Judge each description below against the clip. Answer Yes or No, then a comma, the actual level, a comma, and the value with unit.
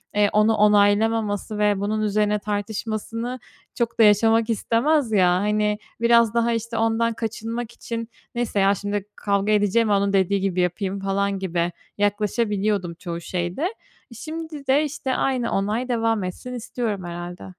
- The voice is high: Yes, high, 210 Hz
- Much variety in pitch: No, narrow, 2.5 semitones